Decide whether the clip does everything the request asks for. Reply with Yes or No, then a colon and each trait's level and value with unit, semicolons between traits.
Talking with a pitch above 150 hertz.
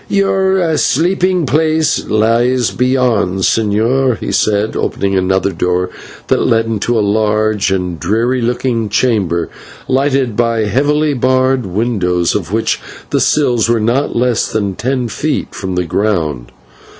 No: low, 115 Hz